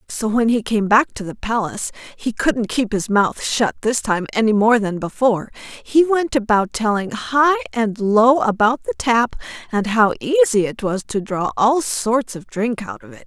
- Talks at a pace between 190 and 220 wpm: Yes, average, 200 wpm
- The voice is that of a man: No, female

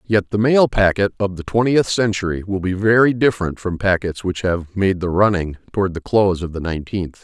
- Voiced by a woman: No, male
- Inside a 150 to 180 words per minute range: No, fast, 205 wpm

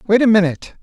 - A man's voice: Yes, male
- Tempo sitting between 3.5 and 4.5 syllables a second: No, 7.5 syllables/s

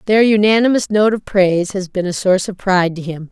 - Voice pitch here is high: Yes, high, 195 Hz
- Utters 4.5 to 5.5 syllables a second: No, 6.0 syllables/s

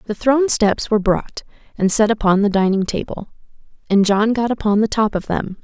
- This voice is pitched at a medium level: No, high, 210 Hz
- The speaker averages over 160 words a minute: Yes, average, 200 wpm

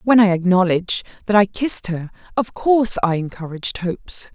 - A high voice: Yes, high, 195 Hz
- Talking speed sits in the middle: Yes, average, 165 wpm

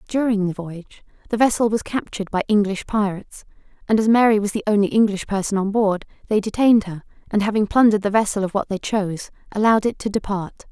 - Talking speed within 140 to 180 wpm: No, average, 200 wpm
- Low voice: No, high, 205 Hz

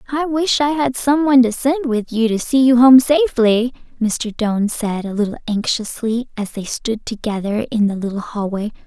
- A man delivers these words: No, female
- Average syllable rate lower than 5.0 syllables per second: No, 5.1 syllables/s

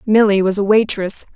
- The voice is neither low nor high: No, high, 205 Hz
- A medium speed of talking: Yes, average, 180 wpm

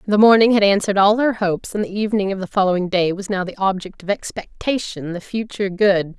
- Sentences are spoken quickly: Yes, fast, 225 wpm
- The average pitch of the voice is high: Yes, high, 200 Hz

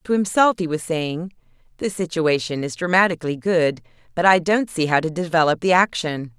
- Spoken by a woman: Yes, female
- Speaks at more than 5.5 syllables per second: No, 5.3 syllables/s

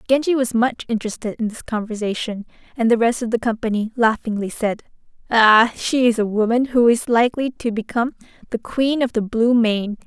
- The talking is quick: No, average, 185 wpm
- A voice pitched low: No, high, 230 Hz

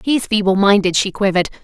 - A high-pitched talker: Yes, high, 200 Hz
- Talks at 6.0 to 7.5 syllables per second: Yes, 6.4 syllables/s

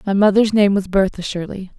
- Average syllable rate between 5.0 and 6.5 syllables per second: Yes, 5.6 syllables/s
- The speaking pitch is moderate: No, high, 195 Hz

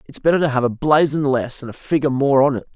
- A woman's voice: No, male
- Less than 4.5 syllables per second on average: No, 7.0 syllables/s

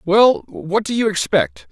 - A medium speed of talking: Yes, average, 175 wpm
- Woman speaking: No, male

